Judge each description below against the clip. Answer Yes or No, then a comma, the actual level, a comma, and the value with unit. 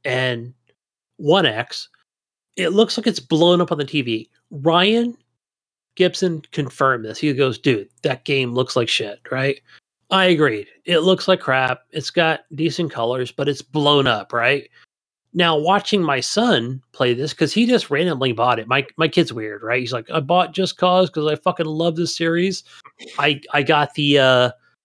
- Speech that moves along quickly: No, average, 175 wpm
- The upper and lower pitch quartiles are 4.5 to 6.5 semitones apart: Yes, average, 5.1 semitones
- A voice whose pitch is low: No, medium, 150 Hz